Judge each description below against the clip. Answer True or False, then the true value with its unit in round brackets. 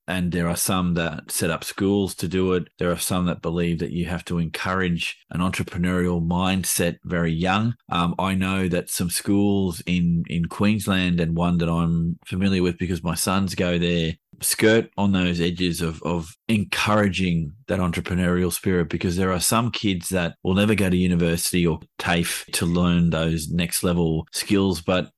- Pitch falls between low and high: False (90 Hz)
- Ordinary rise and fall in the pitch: False (1.7 semitones)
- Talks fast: False (180 wpm)